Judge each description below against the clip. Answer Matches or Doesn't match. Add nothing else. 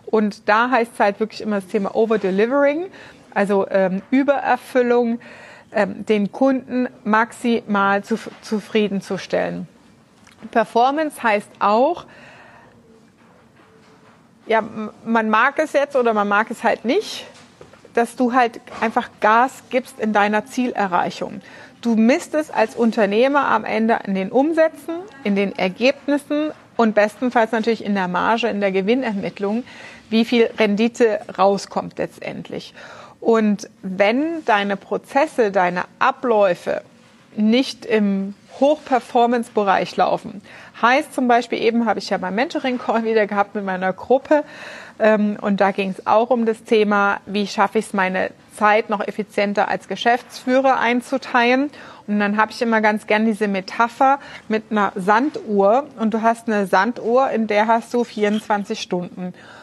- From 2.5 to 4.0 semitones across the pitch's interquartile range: Matches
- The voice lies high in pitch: Matches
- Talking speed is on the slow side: Doesn't match